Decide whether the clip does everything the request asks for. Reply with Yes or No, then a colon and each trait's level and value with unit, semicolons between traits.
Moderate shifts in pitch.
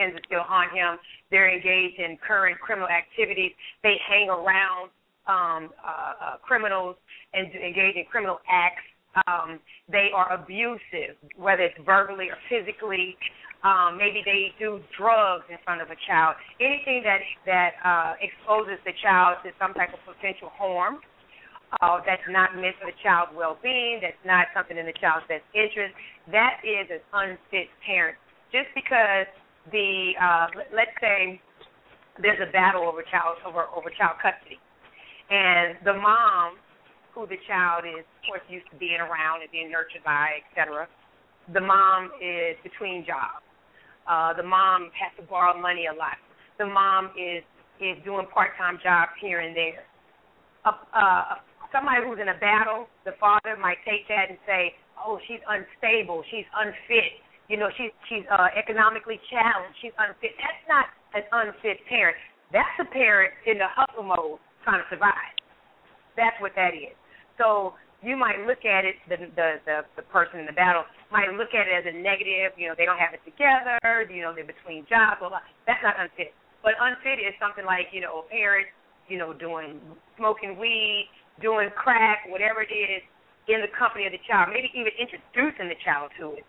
Yes: average, 3.5 semitones